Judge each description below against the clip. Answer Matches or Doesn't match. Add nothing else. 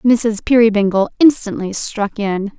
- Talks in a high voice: Matches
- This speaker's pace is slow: Matches